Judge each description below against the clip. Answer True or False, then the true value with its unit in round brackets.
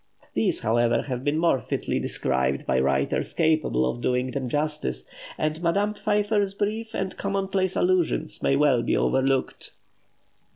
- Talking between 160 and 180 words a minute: False (140 wpm)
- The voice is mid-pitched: True (150 Hz)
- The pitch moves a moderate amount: False (7.9 semitones)